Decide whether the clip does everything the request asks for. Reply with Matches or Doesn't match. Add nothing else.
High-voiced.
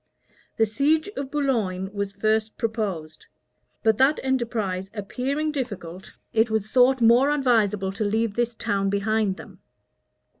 Matches